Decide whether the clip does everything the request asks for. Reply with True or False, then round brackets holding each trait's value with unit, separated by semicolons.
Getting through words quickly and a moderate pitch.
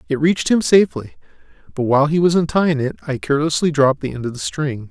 True (220 wpm; 145 Hz)